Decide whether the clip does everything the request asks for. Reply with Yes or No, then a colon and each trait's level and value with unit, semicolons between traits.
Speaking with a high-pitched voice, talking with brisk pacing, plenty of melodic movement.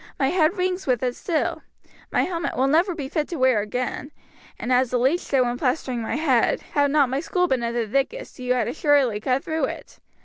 No: very high, 270 Hz; fast, 225 wpm; average, 4.2 semitones